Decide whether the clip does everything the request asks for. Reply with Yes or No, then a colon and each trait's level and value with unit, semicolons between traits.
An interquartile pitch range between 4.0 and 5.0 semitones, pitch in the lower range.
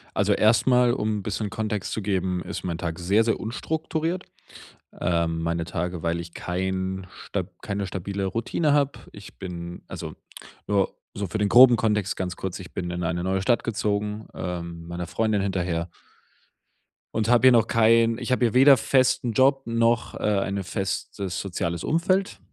Yes: average, 4.5 semitones; low, 100 Hz